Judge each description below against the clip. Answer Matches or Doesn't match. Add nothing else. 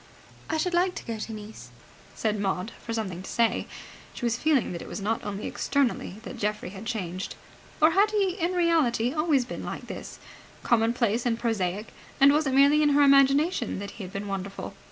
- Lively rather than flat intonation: Matches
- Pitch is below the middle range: Doesn't match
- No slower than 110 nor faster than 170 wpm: Doesn't match